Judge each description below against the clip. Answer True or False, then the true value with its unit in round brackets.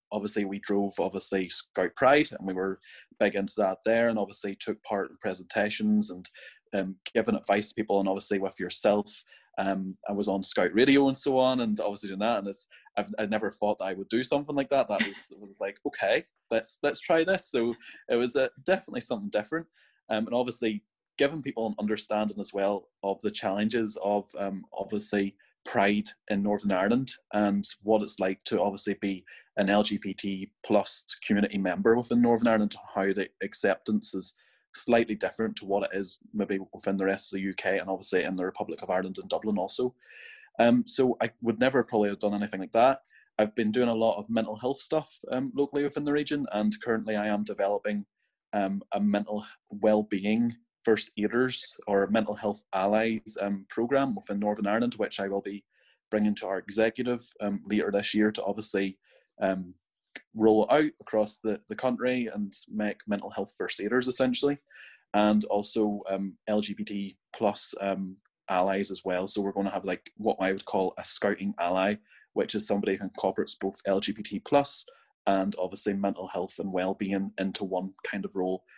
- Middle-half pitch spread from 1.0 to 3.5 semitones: True (2.7 semitones)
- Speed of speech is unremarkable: True (190 wpm)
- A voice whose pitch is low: True (105 Hz)